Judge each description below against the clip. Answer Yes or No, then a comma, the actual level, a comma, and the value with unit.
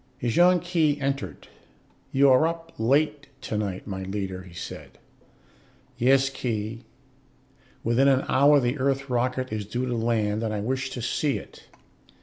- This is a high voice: No, low, 130 Hz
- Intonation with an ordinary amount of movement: Yes, average, 4.2 semitones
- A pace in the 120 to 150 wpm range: Yes, average, 145 wpm